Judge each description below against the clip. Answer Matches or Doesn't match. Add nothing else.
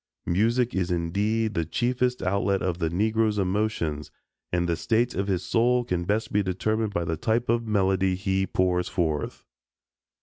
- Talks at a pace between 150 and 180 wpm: Matches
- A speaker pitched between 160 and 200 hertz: Doesn't match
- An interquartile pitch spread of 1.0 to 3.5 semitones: Doesn't match